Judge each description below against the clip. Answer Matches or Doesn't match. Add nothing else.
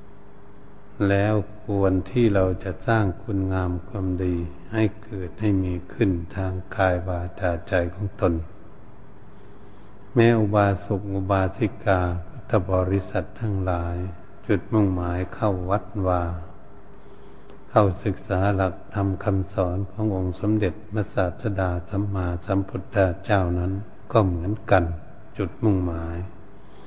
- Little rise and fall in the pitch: Matches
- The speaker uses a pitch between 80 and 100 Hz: Matches